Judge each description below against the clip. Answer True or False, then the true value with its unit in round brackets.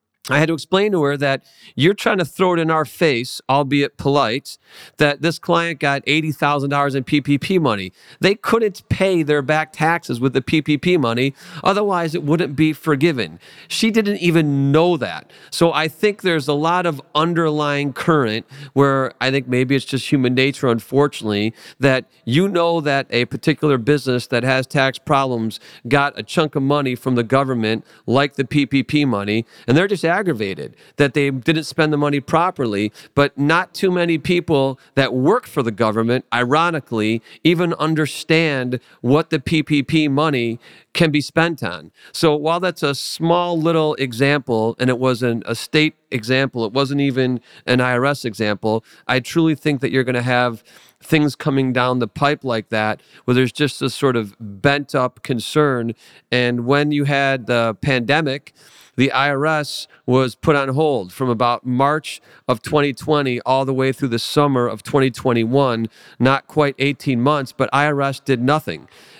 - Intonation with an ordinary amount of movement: True (3.6 semitones)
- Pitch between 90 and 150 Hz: True (140 Hz)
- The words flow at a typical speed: True (170 wpm)